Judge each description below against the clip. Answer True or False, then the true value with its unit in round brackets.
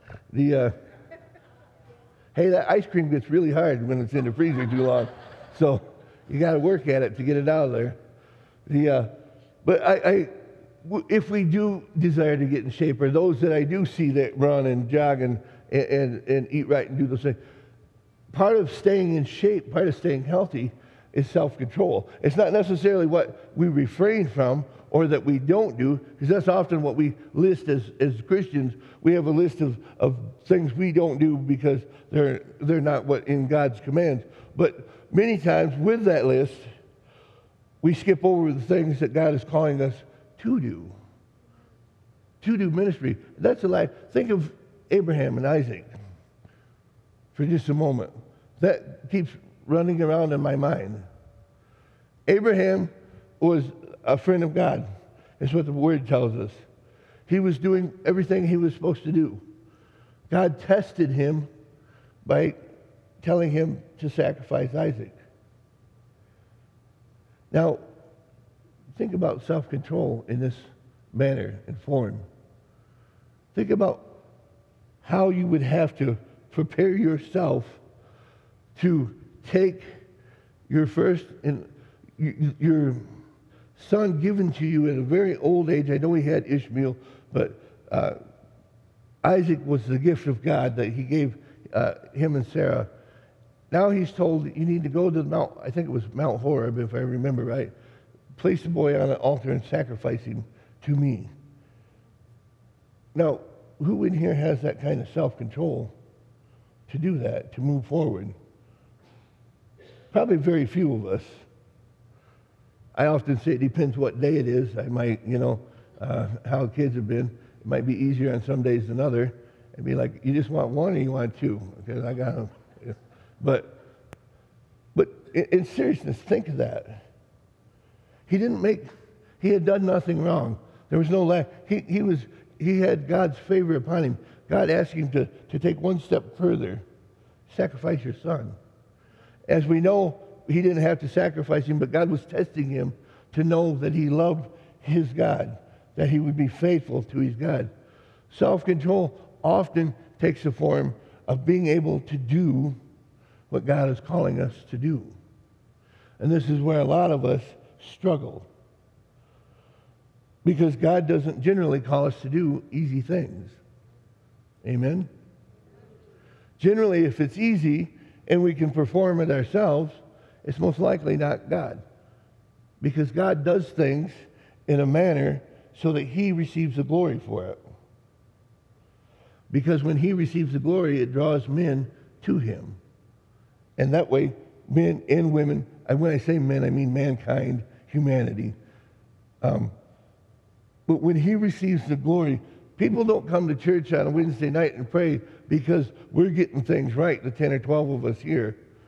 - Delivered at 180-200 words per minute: False (155 wpm)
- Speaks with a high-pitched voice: False (140 Hz)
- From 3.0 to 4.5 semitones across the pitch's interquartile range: False (5.3 semitones)